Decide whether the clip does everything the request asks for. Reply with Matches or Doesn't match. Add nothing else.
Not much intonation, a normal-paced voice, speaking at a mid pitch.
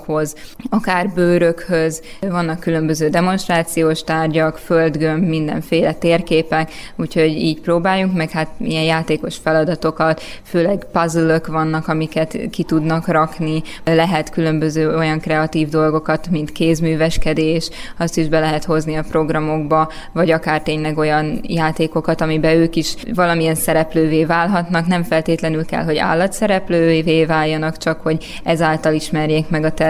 Matches